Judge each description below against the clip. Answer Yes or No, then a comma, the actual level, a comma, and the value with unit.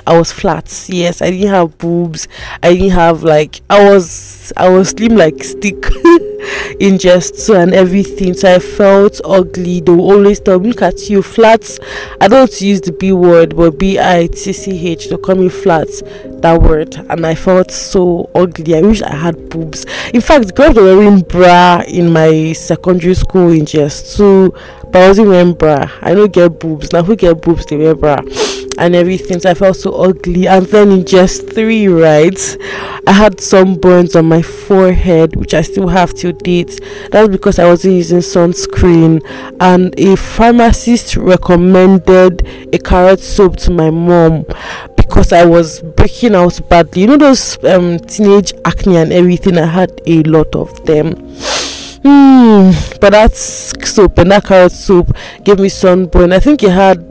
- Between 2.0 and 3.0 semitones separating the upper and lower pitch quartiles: Yes, narrow, 2.6 semitones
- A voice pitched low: No, medium, 185 Hz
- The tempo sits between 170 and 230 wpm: Yes, average, 180 wpm